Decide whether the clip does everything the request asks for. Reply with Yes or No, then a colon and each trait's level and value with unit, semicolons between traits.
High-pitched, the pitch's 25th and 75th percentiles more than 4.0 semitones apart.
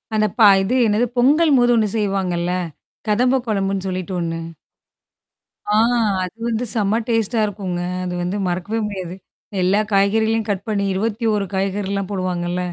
No: high, 200 Hz; average, 3.0 semitones